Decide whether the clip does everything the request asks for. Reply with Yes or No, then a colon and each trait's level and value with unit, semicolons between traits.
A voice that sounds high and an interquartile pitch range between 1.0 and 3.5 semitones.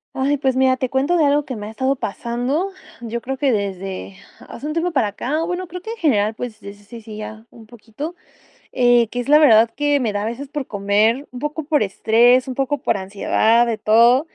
No: high, 245 Hz; average, 4.7 semitones